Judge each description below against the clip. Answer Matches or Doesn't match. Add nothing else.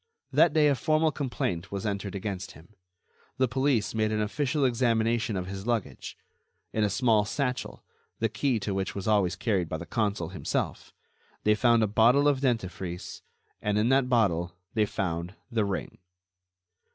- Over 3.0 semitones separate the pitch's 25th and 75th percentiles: Matches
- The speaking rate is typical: Matches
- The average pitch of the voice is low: Matches